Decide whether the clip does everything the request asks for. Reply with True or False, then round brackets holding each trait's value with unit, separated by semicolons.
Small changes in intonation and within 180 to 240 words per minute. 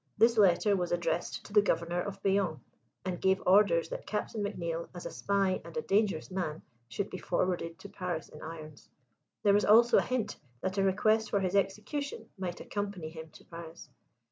False (3.3 semitones; 190 wpm)